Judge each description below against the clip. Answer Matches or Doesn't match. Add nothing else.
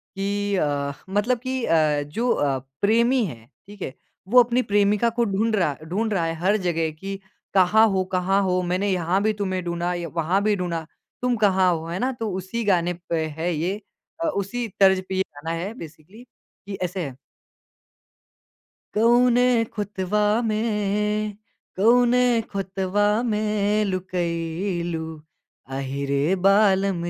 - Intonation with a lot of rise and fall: Doesn't match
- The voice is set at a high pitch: Matches